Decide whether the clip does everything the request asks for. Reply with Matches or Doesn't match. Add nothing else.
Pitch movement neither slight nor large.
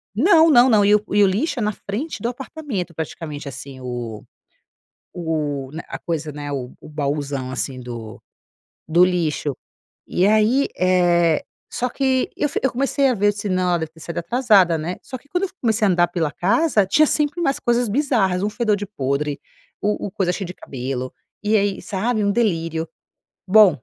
Doesn't match